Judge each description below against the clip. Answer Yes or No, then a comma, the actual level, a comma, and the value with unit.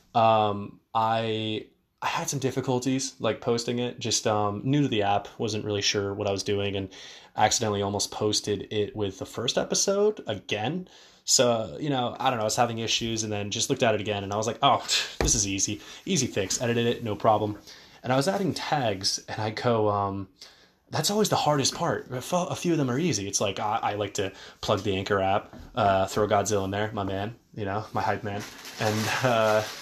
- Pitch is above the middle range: No, low, 110 Hz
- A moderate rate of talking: No, fast, 215 wpm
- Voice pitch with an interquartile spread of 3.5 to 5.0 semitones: Yes, average, 4.2 semitones